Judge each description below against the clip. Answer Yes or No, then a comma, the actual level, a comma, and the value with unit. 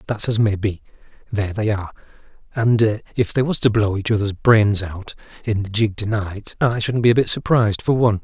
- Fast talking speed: Yes, fast, 220 wpm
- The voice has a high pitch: No, low, 105 Hz